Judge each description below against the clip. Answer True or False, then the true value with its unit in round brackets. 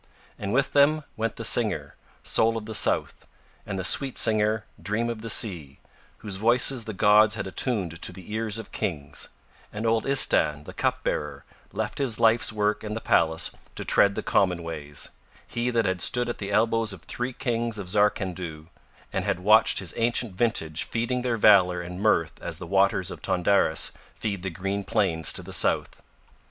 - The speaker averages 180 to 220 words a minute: True (185 wpm)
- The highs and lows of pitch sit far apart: False (4.0 semitones)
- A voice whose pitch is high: False (105 Hz)